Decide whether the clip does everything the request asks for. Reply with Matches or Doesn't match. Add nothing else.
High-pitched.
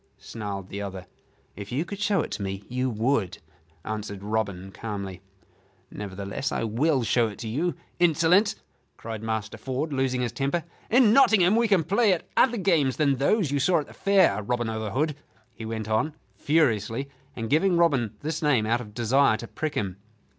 Doesn't match